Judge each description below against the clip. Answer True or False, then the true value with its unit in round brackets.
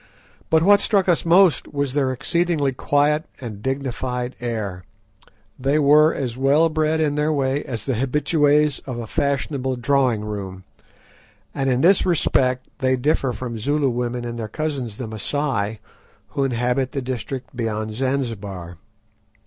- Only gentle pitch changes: False (3.7 semitones)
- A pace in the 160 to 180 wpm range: False (150 wpm)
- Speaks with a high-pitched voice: False (130 Hz)